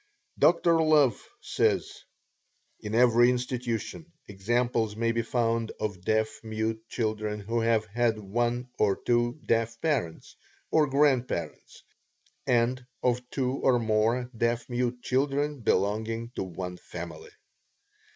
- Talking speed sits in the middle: No, slow, 120 wpm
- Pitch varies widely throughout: No, narrow, 2.4 semitones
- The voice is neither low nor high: No, low, 115 Hz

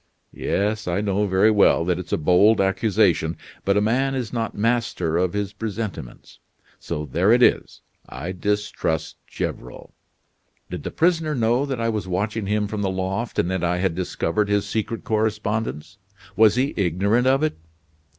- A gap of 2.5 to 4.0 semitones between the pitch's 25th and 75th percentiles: Yes, average, 3.3 semitones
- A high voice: No, low, 105 Hz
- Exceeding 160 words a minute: Yes, average, 170 wpm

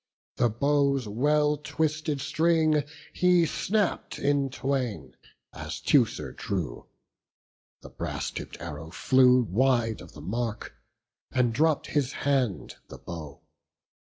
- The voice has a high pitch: No, low, 135 Hz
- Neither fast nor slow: No, slow, 115 wpm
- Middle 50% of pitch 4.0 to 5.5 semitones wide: Yes, average, 4.8 semitones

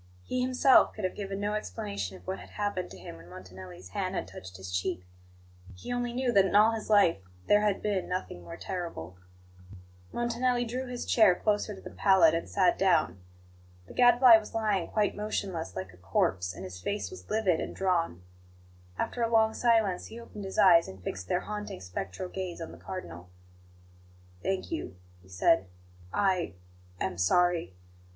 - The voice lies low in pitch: No, medium, 185 Hz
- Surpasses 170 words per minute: Yes, average, 180 wpm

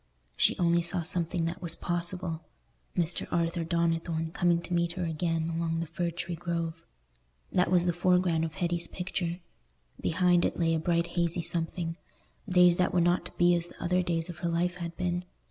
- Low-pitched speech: No, medium, 170 Hz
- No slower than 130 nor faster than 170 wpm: No, average, 185 wpm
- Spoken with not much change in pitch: Yes, narrow, 1.1 semitones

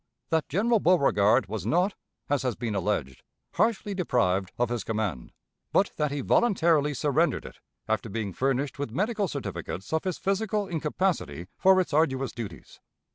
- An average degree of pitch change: No, wide, 8.9 semitones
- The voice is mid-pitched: Yes, medium, 145 Hz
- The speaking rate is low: No, average, 155 wpm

